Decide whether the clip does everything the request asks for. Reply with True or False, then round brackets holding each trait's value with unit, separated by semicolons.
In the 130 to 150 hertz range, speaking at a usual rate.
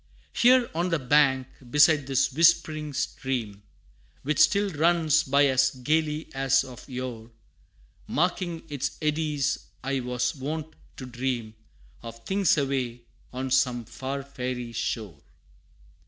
False (135 Hz; 125 wpm)